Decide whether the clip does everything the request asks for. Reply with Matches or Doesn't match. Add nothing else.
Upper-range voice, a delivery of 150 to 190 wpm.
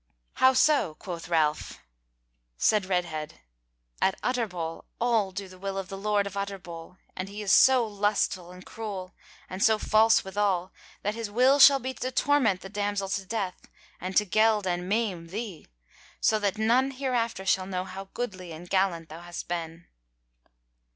Matches